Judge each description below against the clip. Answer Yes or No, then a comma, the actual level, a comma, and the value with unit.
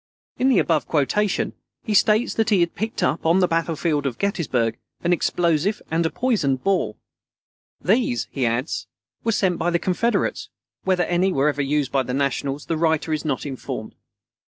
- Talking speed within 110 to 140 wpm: No, average, 180 wpm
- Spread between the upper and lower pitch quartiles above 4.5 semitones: Yes, wide, 5.4 semitones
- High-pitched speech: No, medium, 165 Hz